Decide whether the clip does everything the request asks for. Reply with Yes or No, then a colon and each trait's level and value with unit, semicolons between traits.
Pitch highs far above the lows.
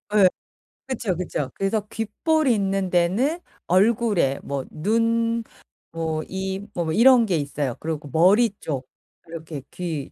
Yes: wide, 6.1 semitones